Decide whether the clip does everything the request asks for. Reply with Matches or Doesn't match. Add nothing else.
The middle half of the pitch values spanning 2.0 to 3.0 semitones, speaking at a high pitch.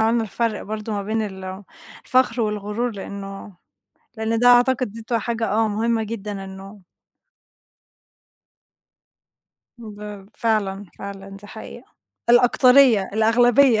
Matches